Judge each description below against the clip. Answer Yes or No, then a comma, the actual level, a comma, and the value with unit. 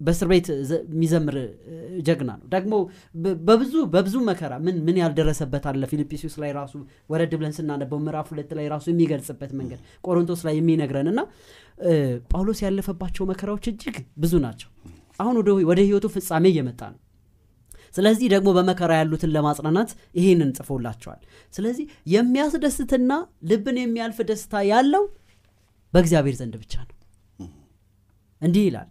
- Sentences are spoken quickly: Yes, fast, 125 wpm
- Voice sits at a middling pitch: Yes, medium, 165 Hz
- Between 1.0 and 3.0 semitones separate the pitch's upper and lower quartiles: No, wide, 5.8 semitones